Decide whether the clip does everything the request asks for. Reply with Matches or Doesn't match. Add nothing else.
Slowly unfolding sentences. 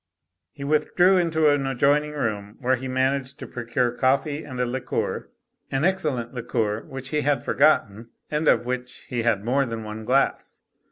Doesn't match